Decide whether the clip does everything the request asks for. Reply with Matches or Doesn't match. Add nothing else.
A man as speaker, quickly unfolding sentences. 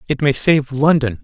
Doesn't match